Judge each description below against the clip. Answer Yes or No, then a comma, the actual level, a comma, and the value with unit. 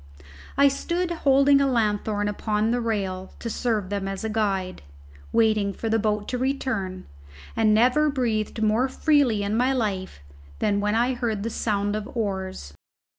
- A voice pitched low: No, high, 220 Hz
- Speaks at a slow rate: No, average, 165 wpm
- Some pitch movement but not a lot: Yes, average, 3.6 semitones